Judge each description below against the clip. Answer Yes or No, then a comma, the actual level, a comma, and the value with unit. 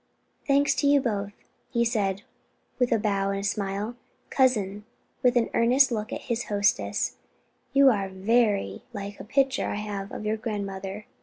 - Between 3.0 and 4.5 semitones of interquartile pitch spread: Yes, average, 3.4 semitones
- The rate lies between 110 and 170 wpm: Yes, average, 160 wpm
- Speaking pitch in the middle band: No, high, 215 Hz